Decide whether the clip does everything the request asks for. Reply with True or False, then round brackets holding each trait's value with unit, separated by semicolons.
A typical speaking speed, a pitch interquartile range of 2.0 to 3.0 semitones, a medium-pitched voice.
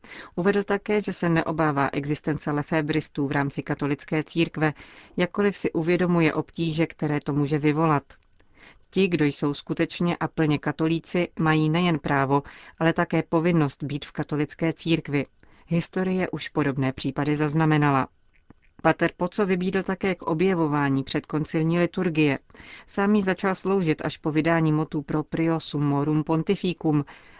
True (130 wpm; 2.6 semitones; 160 Hz)